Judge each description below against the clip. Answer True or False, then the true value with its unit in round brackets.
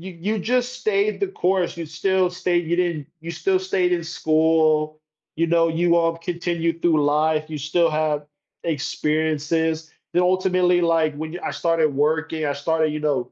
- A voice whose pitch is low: False (165 Hz)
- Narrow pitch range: True (2.3 semitones)